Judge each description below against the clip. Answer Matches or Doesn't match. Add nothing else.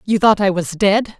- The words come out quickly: Matches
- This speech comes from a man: Matches